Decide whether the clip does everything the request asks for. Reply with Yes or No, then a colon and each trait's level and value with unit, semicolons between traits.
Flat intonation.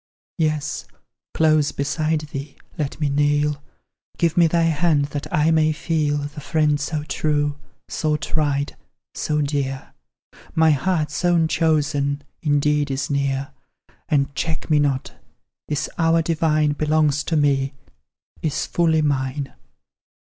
Yes: narrow, 1.7 semitones